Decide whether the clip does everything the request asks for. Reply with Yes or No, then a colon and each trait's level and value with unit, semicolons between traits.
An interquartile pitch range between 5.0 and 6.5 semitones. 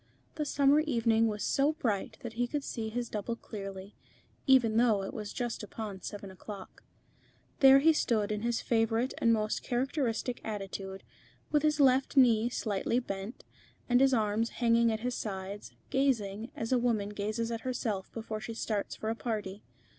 No: average, 3.0 semitones